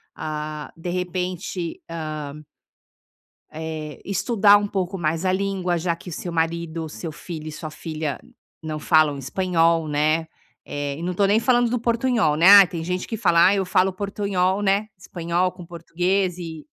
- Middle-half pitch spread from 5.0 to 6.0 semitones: No, average, 3.3 semitones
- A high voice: No, medium, 175 Hz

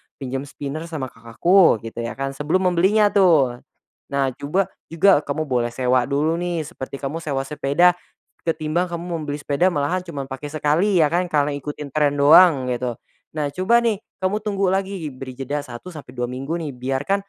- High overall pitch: No, medium, 150 Hz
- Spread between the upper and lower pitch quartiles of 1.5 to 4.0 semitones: No, average, 4.6 semitones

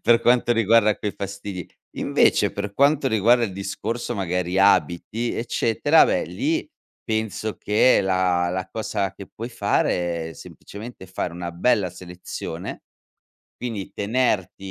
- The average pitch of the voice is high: No, low, 100 Hz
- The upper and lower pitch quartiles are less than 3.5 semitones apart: No, average, 4.1 semitones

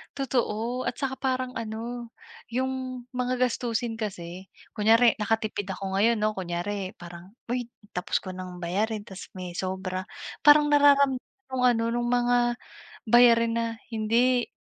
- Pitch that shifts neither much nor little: Yes, average, 4.2 semitones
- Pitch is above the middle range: Yes, high, 230 Hz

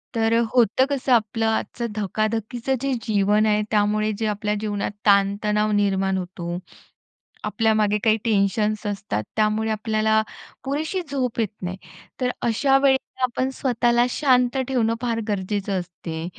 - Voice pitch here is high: Yes, high, 215 Hz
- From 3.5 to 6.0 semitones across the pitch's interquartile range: No, average, 2.7 semitones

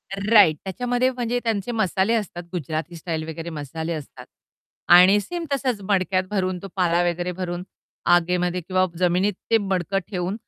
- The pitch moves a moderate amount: Yes, average, 3.0 semitones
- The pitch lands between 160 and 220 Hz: Yes, medium, 185 Hz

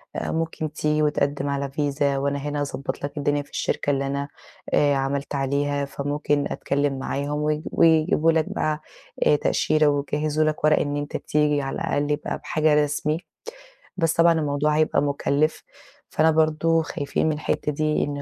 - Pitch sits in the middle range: Yes, medium, 145 Hz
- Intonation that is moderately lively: No, narrow, 1.4 semitones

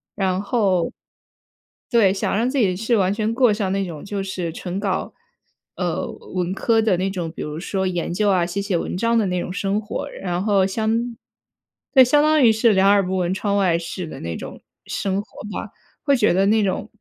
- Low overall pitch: No, high, 195 Hz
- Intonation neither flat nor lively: Yes, average, 3.1 semitones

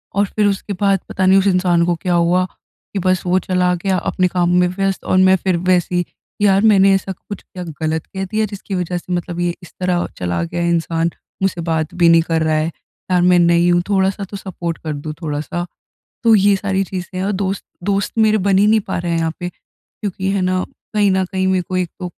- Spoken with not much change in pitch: Yes, narrow, 2.0 semitones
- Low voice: No, medium, 185 Hz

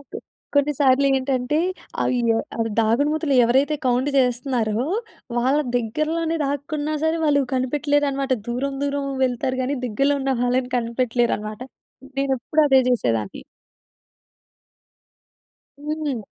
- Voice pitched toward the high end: Yes, very high, 265 Hz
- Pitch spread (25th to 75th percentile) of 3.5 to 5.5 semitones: No, average, 2.8 semitones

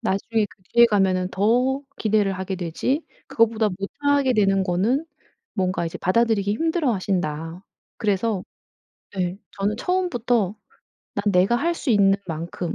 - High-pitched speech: Yes, high, 205 Hz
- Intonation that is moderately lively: Yes, average, 4.2 semitones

